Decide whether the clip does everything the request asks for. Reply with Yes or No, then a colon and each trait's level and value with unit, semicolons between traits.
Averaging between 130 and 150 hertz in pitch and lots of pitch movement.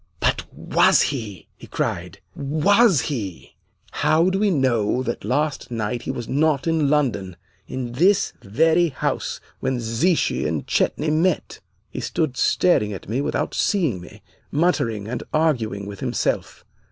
Yes: low, 135 Hz; wide, 5.9 semitones